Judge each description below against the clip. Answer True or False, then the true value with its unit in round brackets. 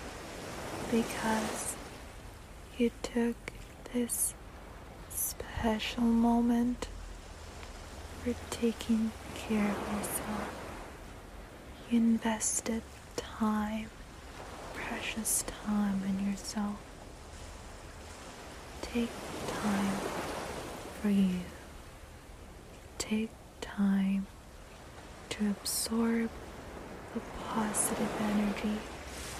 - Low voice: False (215 Hz)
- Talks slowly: True (60 wpm)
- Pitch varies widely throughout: False (4.1 semitones)